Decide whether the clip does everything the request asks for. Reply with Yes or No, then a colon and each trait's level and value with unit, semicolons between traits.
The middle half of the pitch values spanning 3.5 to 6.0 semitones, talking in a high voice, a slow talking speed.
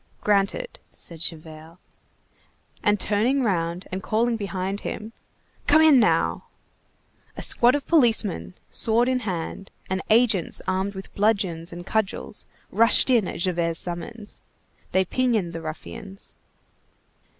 Yes: average, 4.8 semitones; high, 200 Hz; slow, 125 wpm